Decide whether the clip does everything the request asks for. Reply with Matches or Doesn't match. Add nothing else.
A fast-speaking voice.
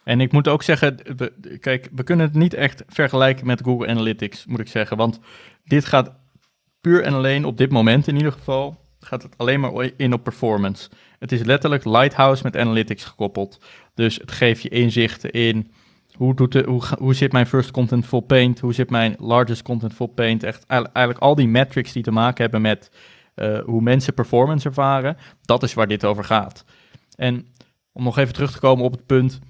Matches